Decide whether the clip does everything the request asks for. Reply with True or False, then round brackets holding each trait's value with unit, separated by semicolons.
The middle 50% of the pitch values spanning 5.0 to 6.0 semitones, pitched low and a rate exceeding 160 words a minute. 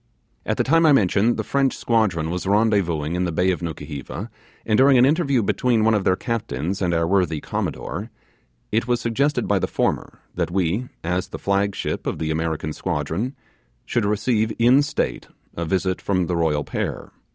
True (5.5 semitones; 100 Hz; 185 wpm)